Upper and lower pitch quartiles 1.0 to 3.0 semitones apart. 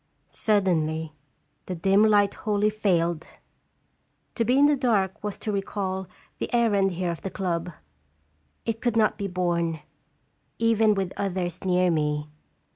No: average, 3.5 semitones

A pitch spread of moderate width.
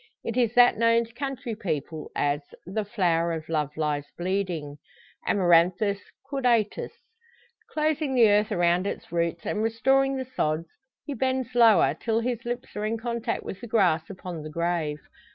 No: wide, 6.1 semitones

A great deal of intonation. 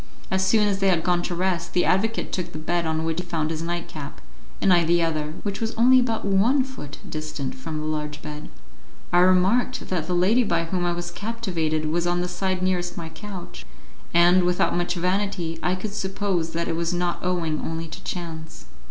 No: average, 2.8 semitones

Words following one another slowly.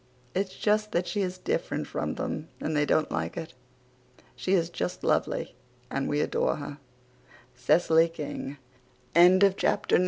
No: average, 150 wpm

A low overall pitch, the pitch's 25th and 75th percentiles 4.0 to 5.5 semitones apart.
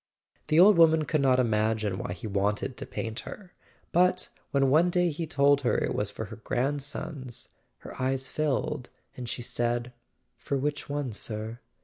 Yes: low, 130 Hz; average, 5.0 semitones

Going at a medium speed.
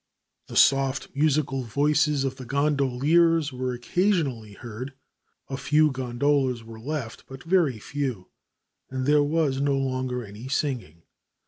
No: slow, 130 wpm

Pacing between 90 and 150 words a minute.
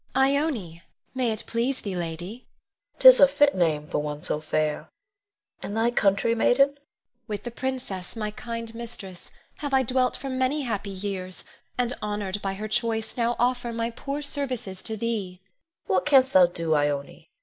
No: average, 175 wpm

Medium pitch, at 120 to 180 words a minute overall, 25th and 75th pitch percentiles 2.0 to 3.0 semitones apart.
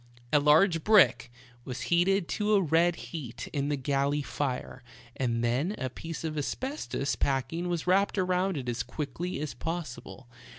No: medium, 150 Hz; average, 160 wpm; average, 5.0 semitones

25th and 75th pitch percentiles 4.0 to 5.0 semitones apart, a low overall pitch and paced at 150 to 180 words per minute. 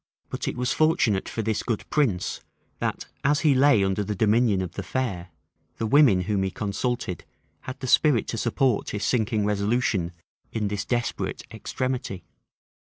Yes: average, 4.3 semitones; low, 110 Hz; average, 160 wpm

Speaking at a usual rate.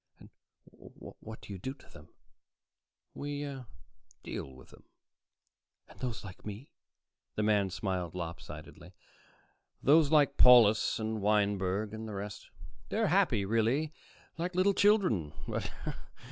No: slow, 120 wpm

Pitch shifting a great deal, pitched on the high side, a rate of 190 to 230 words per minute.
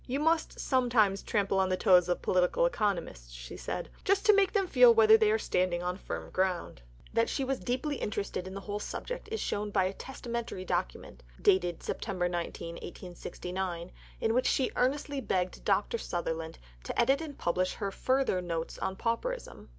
No: wide, 6.9 semitones; high, 200 Hz; average, 180 wpm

